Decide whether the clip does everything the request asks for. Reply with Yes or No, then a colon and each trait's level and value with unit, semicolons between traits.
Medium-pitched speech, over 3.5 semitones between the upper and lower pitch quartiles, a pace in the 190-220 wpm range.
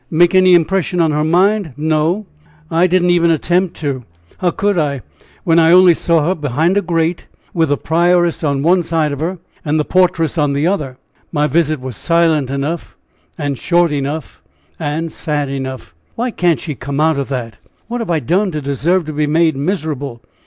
No: medium, 160 Hz; average, 3.2 semitones; average, 195 wpm